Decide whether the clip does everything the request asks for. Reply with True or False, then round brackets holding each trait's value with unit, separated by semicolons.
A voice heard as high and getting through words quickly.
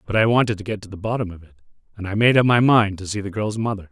False (105 Hz; 320 wpm)